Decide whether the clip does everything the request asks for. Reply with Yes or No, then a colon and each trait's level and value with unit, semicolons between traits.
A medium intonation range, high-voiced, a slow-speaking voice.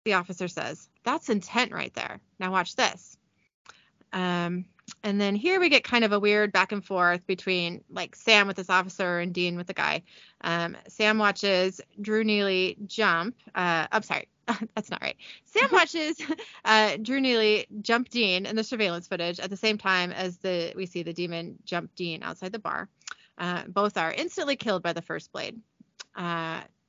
No: average, 3.7 semitones; high, 195 Hz; average, 185 wpm